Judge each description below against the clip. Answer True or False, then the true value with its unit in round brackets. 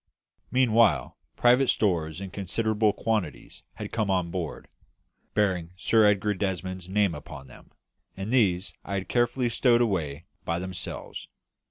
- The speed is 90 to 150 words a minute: True (140 wpm)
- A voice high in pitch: False (100 Hz)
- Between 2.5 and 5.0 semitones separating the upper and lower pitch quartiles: True (3.9 semitones)